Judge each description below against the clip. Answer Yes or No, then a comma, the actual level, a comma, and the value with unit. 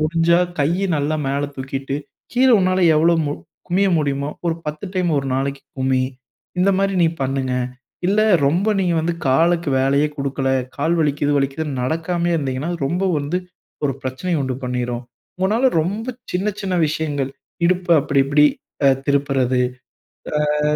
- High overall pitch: No, medium, 150 Hz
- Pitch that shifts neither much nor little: Yes, average, 4.2 semitones